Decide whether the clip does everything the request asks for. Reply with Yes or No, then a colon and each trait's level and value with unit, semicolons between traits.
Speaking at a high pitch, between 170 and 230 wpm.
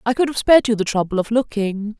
No: high, 220 Hz; fast, 270 wpm